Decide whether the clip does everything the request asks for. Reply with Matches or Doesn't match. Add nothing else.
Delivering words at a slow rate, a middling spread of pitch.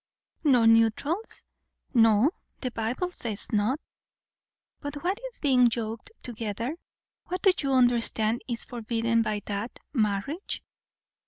Matches